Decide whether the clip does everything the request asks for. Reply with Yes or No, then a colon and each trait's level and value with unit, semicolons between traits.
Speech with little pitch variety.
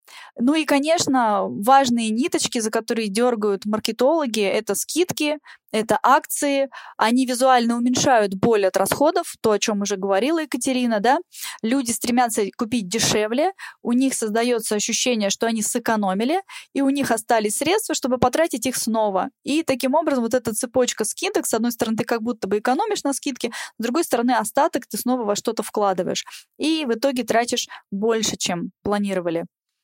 No: average, 4.2 semitones